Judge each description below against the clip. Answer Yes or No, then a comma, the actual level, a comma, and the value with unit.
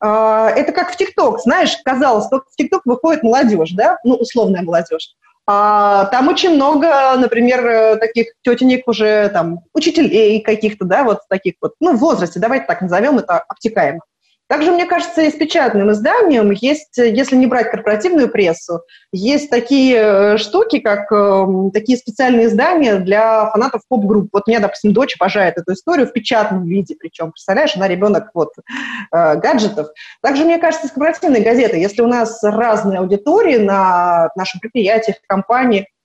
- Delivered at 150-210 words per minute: Yes, fast, 160 wpm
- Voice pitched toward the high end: Yes, high, 225 Hz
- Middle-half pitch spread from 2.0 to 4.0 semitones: No, average, 4.9 semitones